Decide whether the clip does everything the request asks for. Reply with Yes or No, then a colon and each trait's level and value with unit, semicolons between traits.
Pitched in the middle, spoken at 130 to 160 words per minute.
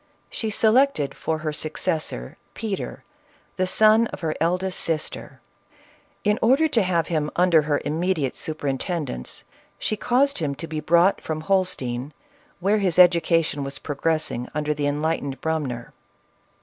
Yes: medium, 160 Hz; average, 140 wpm